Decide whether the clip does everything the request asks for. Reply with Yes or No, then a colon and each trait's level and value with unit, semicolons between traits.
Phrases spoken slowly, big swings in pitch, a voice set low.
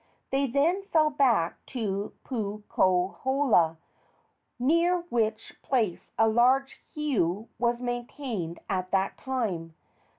No: slow, 100 wpm; wide, 5.8 semitones; high, 235 Hz